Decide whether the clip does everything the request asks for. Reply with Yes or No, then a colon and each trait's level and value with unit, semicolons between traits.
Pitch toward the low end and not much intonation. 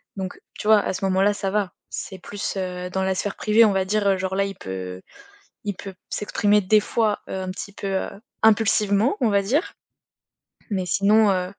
No: high, 195 Hz; narrow, 1.8 semitones